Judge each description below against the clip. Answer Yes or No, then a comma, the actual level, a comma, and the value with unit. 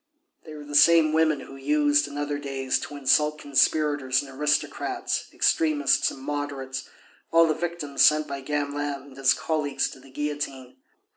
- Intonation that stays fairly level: Yes, narrow, 1.7 semitones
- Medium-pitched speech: Yes, medium, 145 Hz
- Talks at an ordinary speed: Yes, average, 160 wpm